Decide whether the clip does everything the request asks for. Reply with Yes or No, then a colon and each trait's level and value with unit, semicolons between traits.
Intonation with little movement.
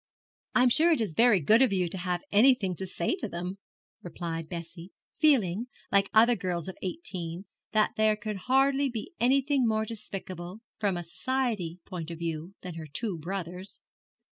No: average, 5.2 semitones